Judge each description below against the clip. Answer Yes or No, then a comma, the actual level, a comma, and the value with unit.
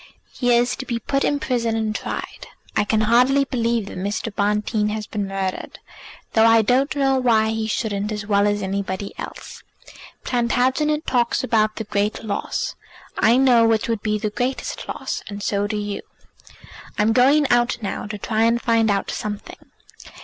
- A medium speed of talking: Yes, average, 175 wpm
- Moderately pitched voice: No, high, 220 Hz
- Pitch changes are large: No, average, 2.7 semitones